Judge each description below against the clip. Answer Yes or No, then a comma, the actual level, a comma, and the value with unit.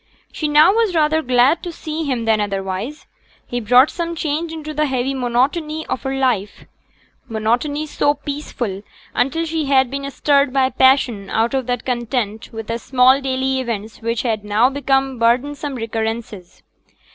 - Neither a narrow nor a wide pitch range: Yes, average, 4.1 semitones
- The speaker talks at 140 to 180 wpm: Yes, average, 160 wpm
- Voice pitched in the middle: No, very high, 260 Hz